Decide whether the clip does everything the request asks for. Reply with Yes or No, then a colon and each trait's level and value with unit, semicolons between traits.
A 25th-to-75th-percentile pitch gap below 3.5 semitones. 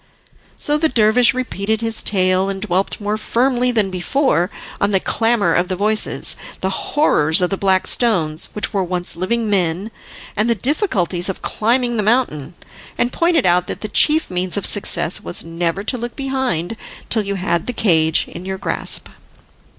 No: average, 4.7 semitones